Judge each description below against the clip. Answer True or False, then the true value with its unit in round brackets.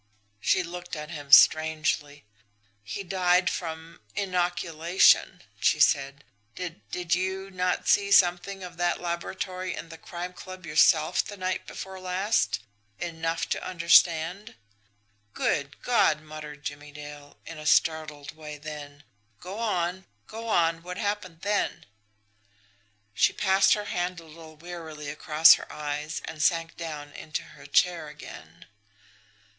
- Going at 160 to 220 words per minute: False (135 wpm)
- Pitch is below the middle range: False (170 Hz)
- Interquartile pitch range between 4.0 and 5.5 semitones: False (3.2 semitones)